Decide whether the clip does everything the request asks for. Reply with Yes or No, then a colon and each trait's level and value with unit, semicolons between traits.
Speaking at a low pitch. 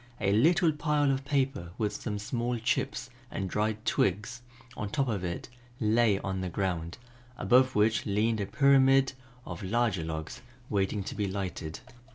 Yes: low, 110 Hz